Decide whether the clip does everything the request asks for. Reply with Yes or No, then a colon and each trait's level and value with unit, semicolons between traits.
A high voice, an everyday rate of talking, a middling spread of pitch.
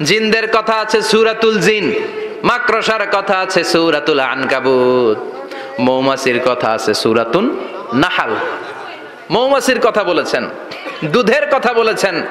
No: high, 215 Hz; average, 100 wpm; wide, 9.0 semitones